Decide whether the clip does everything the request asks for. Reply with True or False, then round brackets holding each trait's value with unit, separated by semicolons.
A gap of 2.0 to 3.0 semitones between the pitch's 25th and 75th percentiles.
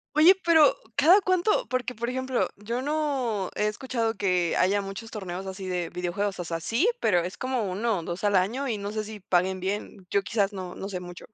False (5.2 semitones)